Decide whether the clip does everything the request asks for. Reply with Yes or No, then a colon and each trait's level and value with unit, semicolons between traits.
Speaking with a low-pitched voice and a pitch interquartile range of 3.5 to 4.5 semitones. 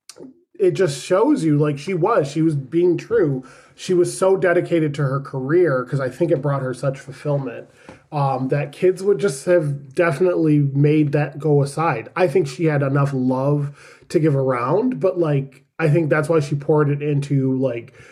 No: medium, 150 Hz; average, 3.8 semitones